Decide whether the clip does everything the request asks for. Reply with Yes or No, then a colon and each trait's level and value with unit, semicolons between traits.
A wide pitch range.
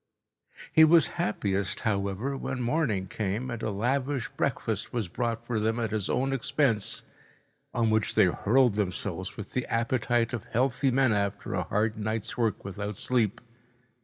No: average, 3.5 semitones